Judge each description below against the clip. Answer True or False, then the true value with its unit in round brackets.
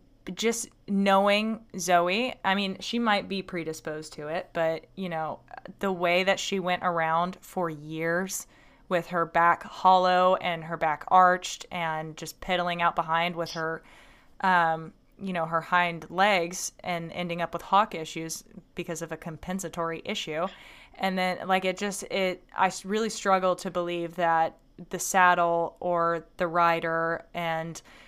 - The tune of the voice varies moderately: False (2.2 semitones)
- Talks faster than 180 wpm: False (155 wpm)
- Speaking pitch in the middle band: True (175 Hz)